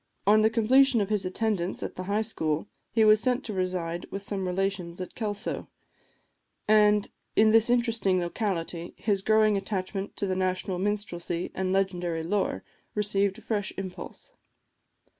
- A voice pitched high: Yes, high, 195 Hz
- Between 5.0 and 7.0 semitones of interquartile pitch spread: No, average, 2.7 semitones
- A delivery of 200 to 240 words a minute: No, average, 155 wpm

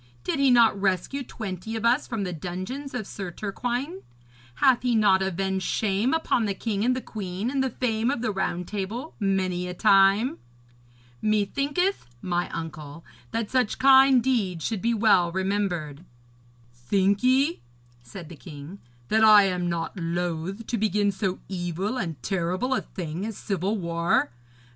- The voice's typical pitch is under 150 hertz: No, high, 200 Hz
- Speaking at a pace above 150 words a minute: Yes, average, 160 wpm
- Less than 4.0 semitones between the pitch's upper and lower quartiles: No, average, 4.7 semitones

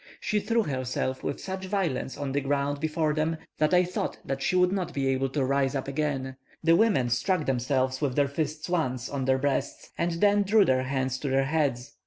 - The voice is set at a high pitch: No, medium, 145 Hz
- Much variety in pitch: No, average, 4.3 semitones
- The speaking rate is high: Yes, fast, 210 wpm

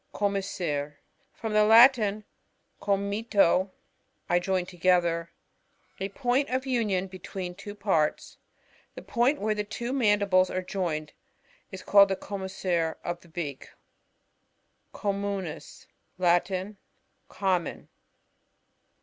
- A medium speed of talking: No, slow, 115 wpm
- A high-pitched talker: Yes, high, 195 Hz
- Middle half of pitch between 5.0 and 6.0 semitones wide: No, average, 2.7 semitones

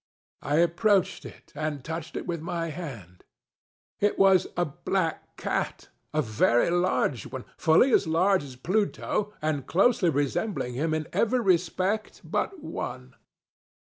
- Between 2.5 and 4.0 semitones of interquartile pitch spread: No, average, 4.6 semitones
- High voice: No, medium, 170 Hz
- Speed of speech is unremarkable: No, slow, 130 wpm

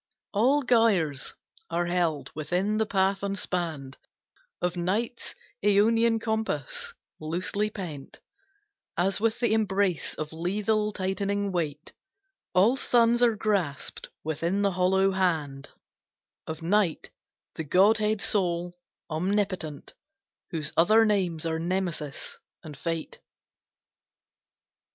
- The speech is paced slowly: Yes, slow, 105 wpm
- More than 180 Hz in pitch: Yes, high, 190 Hz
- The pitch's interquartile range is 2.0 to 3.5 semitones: No, average, 4.3 semitones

